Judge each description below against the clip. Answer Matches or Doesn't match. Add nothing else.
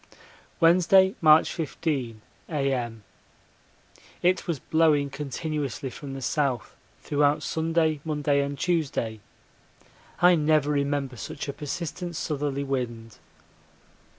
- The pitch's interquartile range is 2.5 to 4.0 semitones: Matches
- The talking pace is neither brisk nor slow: Doesn't match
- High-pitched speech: Doesn't match